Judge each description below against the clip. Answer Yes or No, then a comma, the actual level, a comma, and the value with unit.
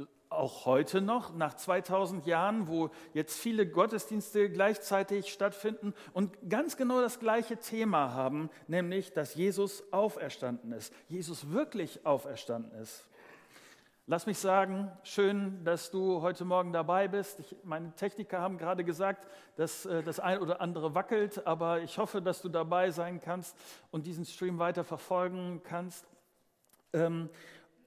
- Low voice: No, medium, 180 Hz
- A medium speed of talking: Yes, average, 140 wpm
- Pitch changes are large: No, average, 3.2 semitones